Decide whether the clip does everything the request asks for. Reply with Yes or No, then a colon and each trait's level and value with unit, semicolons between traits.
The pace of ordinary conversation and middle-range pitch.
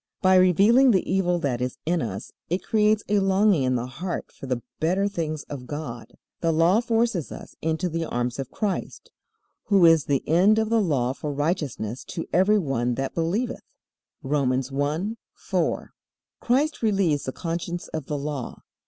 Yes: average, 170 wpm; medium, 165 Hz